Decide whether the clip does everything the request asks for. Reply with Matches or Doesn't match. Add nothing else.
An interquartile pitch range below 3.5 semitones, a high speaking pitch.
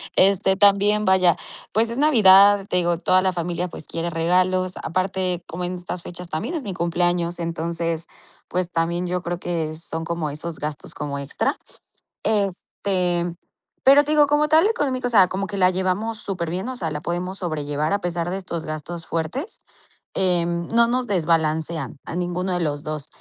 Doesn't match